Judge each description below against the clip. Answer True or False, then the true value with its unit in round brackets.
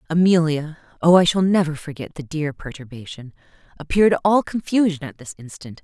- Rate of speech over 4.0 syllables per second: False (3.7 syllables/s)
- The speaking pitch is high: False (160 Hz)